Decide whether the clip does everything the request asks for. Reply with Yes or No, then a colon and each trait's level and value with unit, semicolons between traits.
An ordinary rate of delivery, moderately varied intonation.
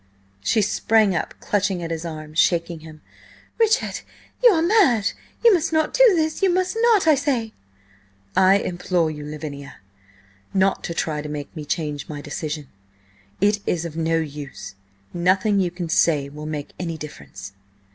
No: average, 165 wpm; wide, 6.5 semitones